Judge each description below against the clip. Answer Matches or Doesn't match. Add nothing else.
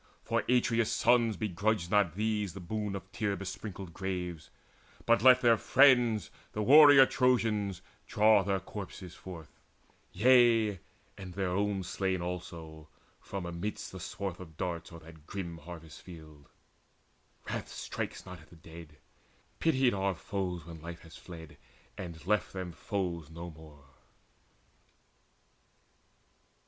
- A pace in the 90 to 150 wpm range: Matches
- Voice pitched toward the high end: Doesn't match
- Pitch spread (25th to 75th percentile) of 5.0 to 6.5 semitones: Doesn't match